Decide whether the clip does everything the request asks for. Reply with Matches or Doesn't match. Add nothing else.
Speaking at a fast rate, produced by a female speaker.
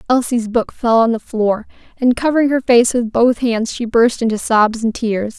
Matches